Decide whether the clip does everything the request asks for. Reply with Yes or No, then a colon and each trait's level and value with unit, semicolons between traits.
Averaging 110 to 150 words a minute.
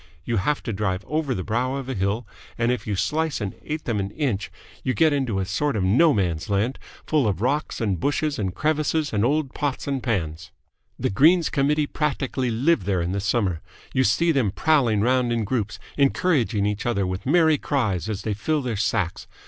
No: fast, 205 wpm